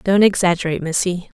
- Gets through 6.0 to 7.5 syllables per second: Yes, 6.2 syllables/s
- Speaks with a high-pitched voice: No, medium, 180 Hz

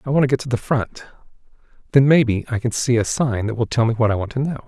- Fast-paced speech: Yes, fast, 295 wpm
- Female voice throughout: No, male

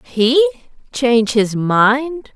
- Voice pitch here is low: No, high, 245 Hz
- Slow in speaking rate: Yes, slow, 100 wpm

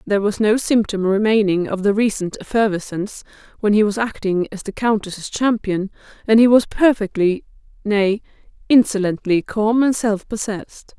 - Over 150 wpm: No, average, 140 wpm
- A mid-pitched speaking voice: No, high, 210 Hz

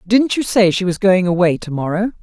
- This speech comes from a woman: Yes, female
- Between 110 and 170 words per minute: No, fast, 245 wpm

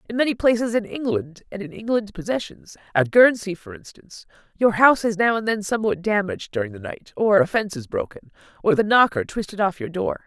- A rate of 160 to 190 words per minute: No, average, 200 wpm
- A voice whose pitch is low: No, high, 205 Hz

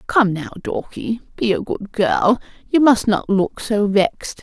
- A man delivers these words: No, female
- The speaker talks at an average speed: Yes, average, 165 wpm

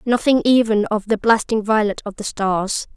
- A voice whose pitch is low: No, high, 215 Hz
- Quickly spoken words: No, average, 180 wpm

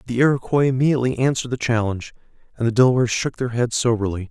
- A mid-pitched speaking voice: No, low, 120 Hz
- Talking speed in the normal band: Yes, average, 180 wpm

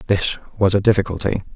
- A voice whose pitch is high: No, low, 100 Hz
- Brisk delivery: No, average, 155 wpm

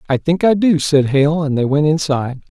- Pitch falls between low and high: Yes, medium, 150 Hz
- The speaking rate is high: Yes, fast, 230 wpm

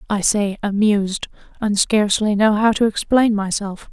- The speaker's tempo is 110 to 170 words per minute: Yes, average, 140 wpm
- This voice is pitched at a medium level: No, high, 210 Hz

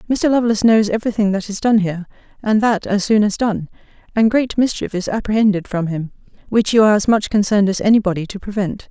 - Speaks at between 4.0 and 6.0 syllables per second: No, 6.5 syllables/s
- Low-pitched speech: No, high, 210 Hz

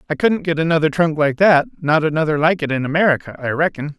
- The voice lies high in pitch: No, medium, 155 Hz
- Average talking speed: No, fast, 210 wpm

